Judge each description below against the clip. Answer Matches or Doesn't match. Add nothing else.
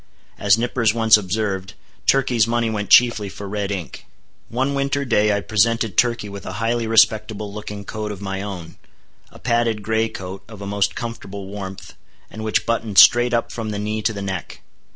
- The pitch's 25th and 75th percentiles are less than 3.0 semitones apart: Matches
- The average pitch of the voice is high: Doesn't match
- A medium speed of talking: Matches